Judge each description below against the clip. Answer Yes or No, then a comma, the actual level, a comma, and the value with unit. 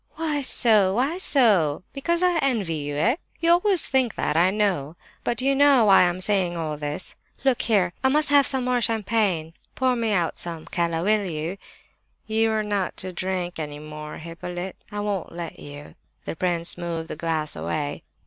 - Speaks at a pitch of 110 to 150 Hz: No, high, 190 Hz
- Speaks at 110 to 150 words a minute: No, average, 185 wpm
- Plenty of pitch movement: Yes, wide, 6.8 semitones